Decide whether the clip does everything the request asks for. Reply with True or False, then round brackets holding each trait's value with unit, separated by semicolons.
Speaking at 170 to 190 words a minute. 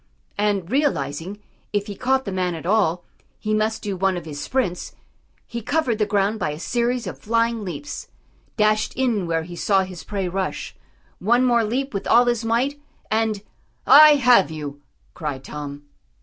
True (175 wpm)